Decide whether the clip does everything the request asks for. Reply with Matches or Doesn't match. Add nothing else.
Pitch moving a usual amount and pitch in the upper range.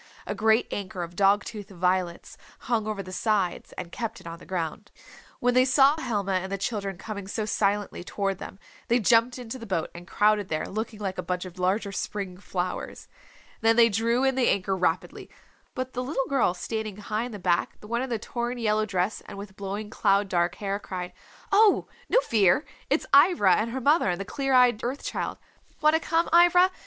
Matches